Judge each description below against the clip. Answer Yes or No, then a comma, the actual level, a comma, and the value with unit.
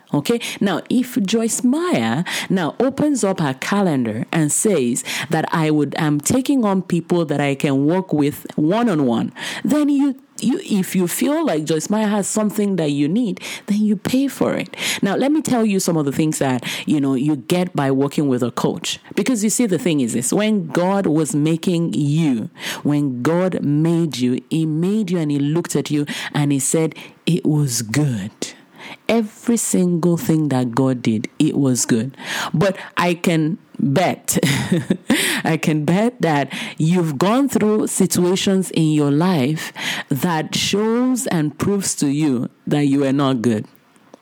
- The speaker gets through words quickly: No, average, 175 wpm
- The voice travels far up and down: Yes, wide, 6.6 semitones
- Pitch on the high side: No, medium, 175 Hz